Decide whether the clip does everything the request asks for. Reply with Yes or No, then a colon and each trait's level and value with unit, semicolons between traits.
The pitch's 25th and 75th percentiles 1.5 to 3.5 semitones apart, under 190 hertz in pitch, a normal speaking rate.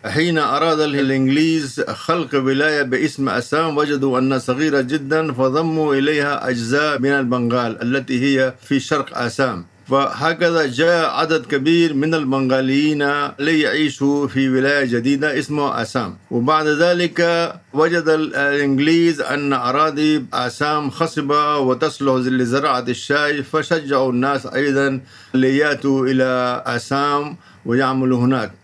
Yes: average, 2.8 semitones; medium, 140 Hz; average, 110 wpm